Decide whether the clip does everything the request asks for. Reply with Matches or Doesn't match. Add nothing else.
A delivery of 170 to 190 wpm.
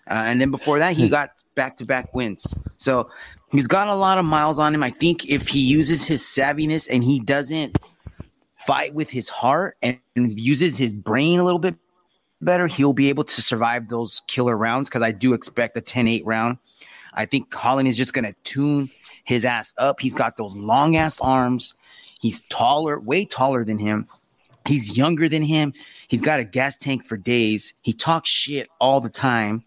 Doesn't match